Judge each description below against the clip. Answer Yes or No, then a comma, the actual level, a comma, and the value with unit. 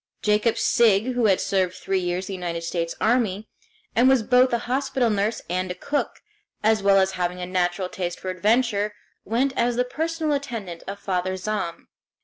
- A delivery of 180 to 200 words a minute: Yes, average, 185 wpm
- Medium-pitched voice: No, high, 205 Hz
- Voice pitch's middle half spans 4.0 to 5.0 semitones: Yes, average, 4.7 semitones